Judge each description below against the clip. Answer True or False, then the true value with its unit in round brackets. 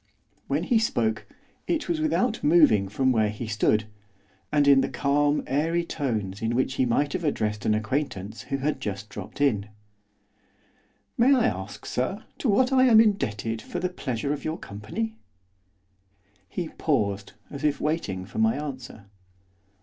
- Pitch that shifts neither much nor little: False (7.6 semitones)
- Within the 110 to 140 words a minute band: False (160 wpm)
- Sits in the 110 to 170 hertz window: True (140 Hz)